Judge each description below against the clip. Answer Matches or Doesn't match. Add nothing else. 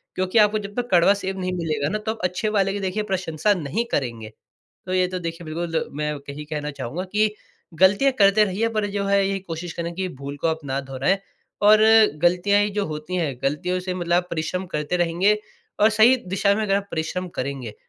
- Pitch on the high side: Doesn't match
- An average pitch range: Matches